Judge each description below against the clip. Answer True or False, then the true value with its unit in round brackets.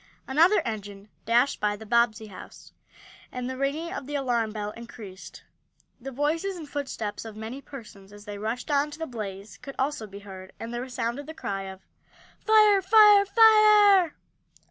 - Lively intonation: True (6.7 semitones)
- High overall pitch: True (245 Hz)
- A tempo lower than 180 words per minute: True (170 wpm)